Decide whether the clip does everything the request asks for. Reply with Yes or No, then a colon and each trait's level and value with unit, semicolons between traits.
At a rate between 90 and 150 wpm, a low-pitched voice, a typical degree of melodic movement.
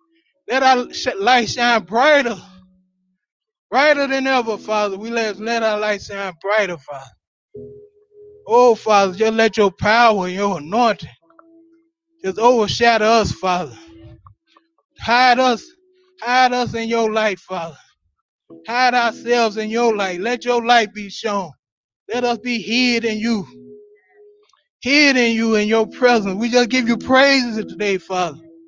No: average, 140 wpm; high, 230 Hz; average, 4.2 semitones